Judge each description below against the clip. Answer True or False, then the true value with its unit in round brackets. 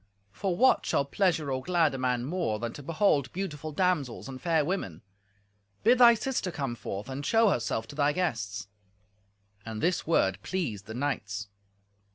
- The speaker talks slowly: False (170 wpm)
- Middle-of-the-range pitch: True (145 Hz)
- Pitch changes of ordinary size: False (7.4 semitones)